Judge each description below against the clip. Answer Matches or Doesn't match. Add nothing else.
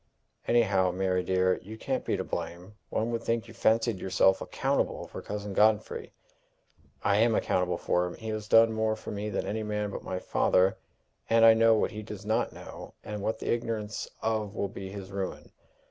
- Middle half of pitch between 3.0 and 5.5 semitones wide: Doesn't match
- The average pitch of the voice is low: Matches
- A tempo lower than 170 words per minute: Doesn't match